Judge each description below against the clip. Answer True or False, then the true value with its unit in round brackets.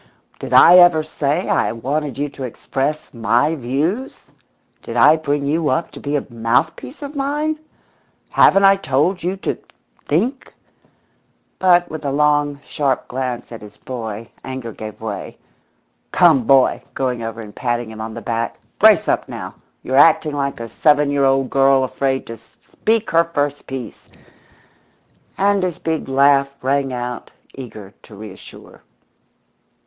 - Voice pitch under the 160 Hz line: True (140 Hz)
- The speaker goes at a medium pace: True (155 wpm)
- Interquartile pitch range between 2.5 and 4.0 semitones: False (4.6 semitones)